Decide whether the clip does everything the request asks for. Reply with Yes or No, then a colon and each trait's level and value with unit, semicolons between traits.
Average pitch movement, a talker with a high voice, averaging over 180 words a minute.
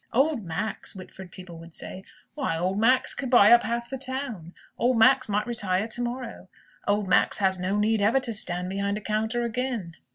Yes: average, 4.2 semitones; high, 215 Hz; average, 195 wpm